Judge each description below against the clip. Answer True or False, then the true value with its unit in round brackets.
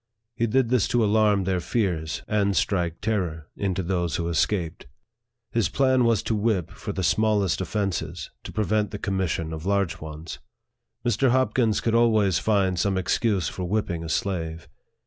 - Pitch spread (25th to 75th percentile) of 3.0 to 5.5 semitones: True (4.0 semitones)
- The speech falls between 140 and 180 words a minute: True (165 wpm)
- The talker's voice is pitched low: True (100 Hz)